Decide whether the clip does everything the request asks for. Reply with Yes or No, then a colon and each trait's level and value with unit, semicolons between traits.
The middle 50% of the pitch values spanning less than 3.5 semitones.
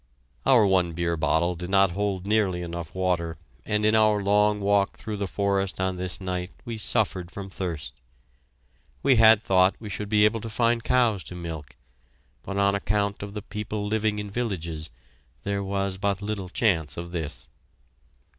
Yes: average, 2.8 semitones